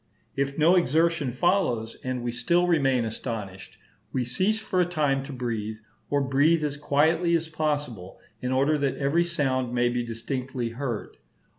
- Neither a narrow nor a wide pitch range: Yes, average, 4.7 semitones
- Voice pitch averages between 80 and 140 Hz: Yes, low, 135 Hz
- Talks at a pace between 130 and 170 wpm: Yes, average, 160 wpm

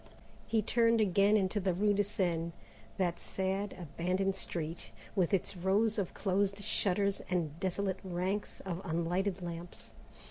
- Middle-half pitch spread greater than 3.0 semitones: No, narrow, 2.5 semitones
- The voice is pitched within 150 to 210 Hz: Yes, high, 190 Hz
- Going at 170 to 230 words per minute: No, average, 140 wpm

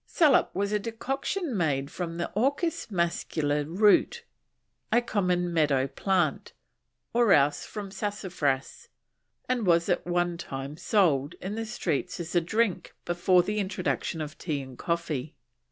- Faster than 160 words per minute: No, average, 140 wpm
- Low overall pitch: No, medium, 175 Hz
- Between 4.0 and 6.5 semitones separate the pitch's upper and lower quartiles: Yes, average, 5.1 semitones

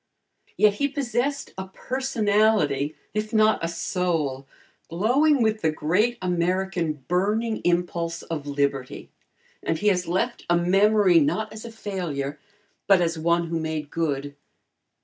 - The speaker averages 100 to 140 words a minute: Yes, slow, 135 wpm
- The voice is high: No, medium, 180 Hz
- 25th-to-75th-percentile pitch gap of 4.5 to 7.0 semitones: Yes, average, 5.1 semitones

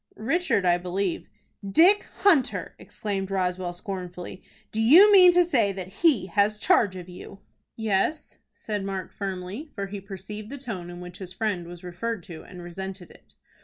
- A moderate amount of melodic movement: Yes, average, 3.6 semitones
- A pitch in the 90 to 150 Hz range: No, high, 195 Hz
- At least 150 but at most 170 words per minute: Yes, average, 165 wpm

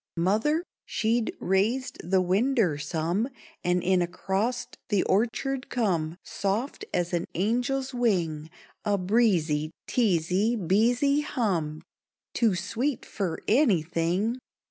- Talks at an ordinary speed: No, slow, 105 wpm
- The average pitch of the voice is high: Yes, high, 200 Hz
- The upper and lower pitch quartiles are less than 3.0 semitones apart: No, wide, 5.5 semitones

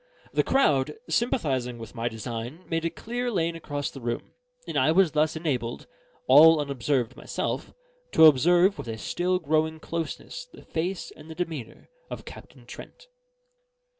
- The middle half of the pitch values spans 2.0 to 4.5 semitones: No, average, 4.9 semitones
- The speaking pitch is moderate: Yes, medium, 155 Hz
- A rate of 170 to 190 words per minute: No, average, 155 wpm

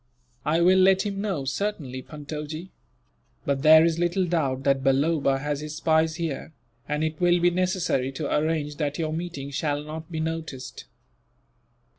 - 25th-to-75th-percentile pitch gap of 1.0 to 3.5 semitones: Yes, average, 2.9 semitones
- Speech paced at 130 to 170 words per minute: Yes, average, 160 wpm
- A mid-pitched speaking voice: Yes, medium, 155 Hz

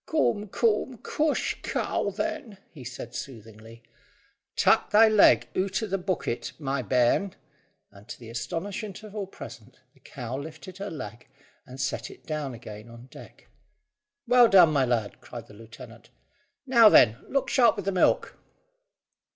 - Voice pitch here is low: No, medium, 155 Hz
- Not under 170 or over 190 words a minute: No, average, 155 wpm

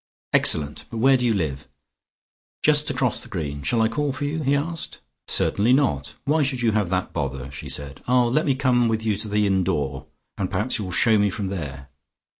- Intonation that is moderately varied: No, wide, 9.0 semitones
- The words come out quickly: Yes, fast, 220 wpm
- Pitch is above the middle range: No, low, 105 Hz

